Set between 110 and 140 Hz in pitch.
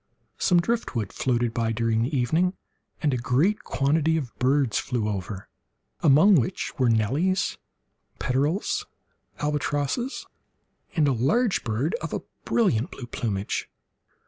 Yes: low, 135 Hz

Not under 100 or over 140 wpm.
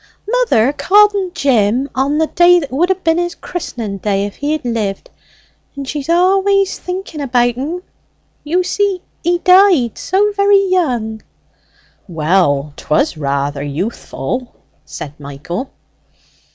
Yes: slow, 135 wpm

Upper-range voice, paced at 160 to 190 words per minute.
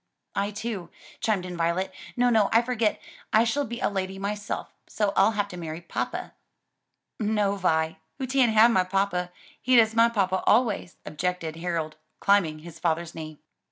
Yes: high, 195 Hz; average, 170 wpm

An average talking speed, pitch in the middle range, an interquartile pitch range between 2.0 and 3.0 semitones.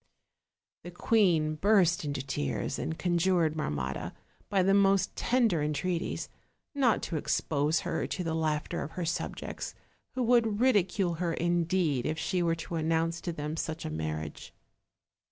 No: average, 150 wpm; medium, 165 Hz; average, 3.6 semitones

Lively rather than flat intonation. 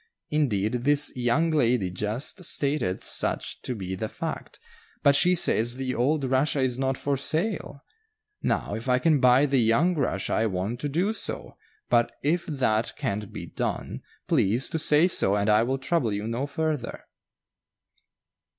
No: average, 4.7 semitones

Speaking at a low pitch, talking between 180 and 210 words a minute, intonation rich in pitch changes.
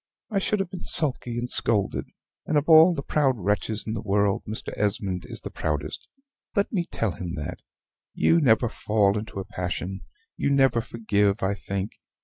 Yes: low, 110 Hz; average, 185 wpm; wide, 5.8 semitones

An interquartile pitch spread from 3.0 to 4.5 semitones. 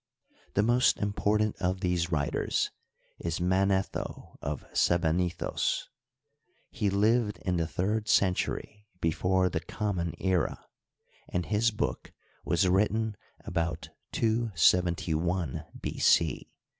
Yes: average, 3.4 semitones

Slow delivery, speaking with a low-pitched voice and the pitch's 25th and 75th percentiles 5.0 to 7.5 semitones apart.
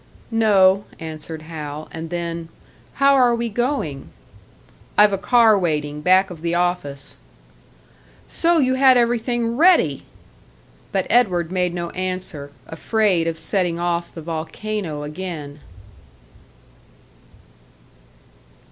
No: slow, 110 wpm; medium, 180 Hz; wide, 5.5 semitones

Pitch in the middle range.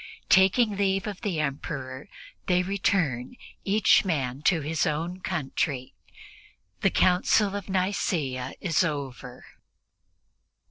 Yes: medium, 175 Hz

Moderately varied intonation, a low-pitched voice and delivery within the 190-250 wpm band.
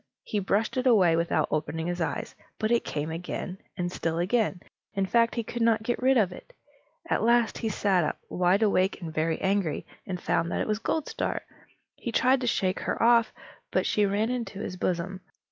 No: average, 4.6 semitones; high, 200 Hz; average, 200 wpm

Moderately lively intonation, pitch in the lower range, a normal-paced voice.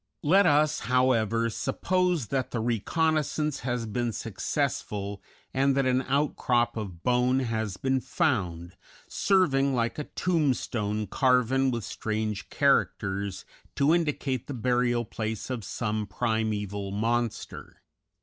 No: average, 4.1 semitones; low, 120 Hz; slow, 120 wpm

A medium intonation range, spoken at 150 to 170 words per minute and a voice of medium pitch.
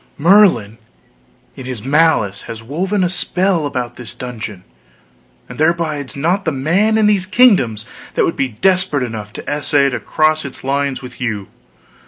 No: wide, 6.6 semitones; average, 165 wpm; medium, 145 Hz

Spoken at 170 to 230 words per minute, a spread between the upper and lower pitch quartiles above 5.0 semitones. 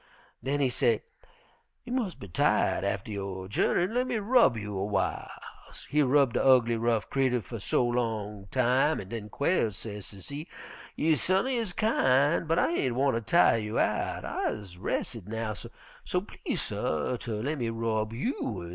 Yes: average, 175 wpm; wide, 5.6 semitones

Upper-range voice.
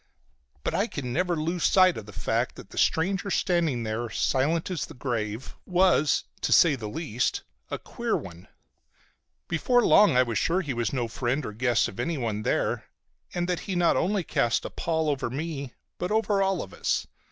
No: medium, 150 Hz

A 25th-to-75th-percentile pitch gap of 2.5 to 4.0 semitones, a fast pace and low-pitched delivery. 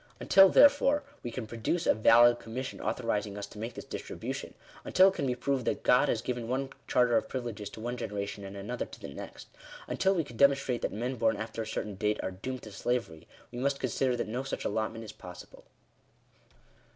Yes: average, 3.3 semitones; fast, 220 wpm; low, 120 Hz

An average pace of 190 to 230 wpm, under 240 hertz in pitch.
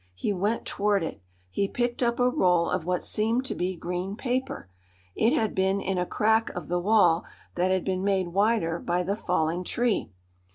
Yes: average, 195 wpm; high, 190 Hz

